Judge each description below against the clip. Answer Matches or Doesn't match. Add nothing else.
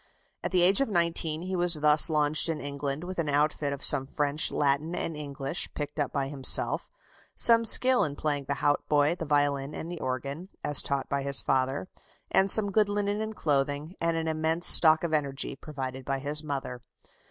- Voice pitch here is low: Doesn't match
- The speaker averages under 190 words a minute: Doesn't match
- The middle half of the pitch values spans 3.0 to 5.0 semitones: Matches